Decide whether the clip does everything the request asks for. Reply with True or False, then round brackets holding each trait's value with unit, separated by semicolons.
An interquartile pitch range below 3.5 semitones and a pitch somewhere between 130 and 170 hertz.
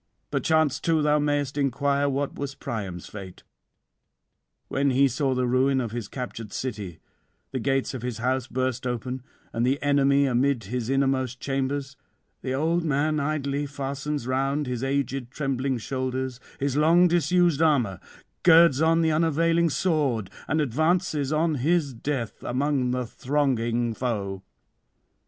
True (2.8 semitones; 135 Hz)